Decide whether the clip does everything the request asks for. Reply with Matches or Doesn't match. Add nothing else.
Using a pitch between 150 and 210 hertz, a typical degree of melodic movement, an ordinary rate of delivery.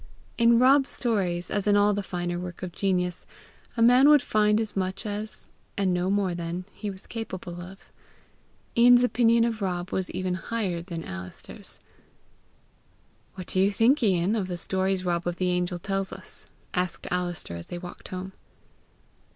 Matches